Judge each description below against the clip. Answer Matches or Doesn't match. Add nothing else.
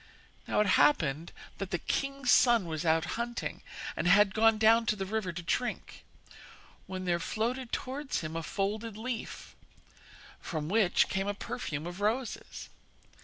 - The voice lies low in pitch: Doesn't match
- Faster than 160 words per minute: Doesn't match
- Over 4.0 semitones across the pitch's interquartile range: Matches